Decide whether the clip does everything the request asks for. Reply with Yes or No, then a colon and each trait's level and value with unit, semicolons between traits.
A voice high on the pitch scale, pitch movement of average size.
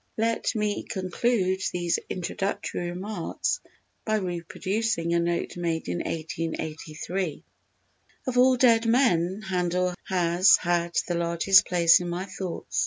No: medium, 180 Hz; average, 3.3 semitones